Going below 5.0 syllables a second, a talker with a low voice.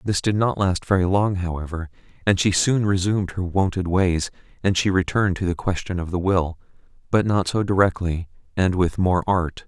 No: 5.2 syllables/s; very low, 90 Hz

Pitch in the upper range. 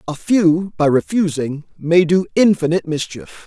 No: medium, 165 Hz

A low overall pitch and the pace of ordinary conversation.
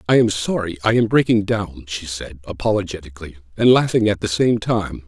Yes: low, 100 Hz; average, 190 wpm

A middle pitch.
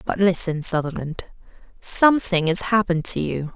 Yes: medium, 180 Hz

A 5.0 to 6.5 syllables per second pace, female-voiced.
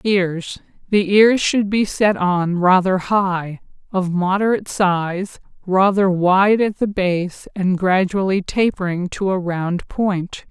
No: 3.5 syllables/s; female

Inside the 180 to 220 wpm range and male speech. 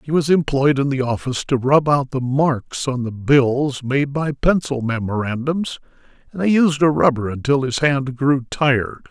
Yes: average, 185 wpm; male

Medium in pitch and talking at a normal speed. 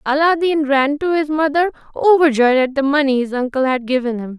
No: very high, 280 Hz; average, 190 wpm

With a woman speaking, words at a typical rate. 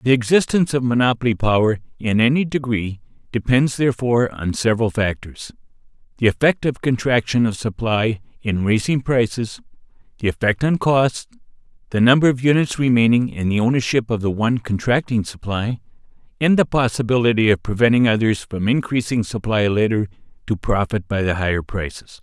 No: male; average, 150 wpm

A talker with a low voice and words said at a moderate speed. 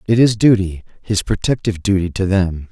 Yes: low, 100 Hz; average, 175 wpm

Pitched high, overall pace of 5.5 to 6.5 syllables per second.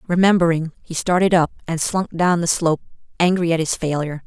No: medium, 170 Hz; 6.0 syllables/s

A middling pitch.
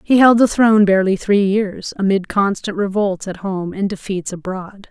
No: high, 200 Hz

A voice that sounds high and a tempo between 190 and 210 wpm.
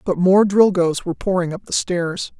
No: medium, 180 Hz; average, 200 wpm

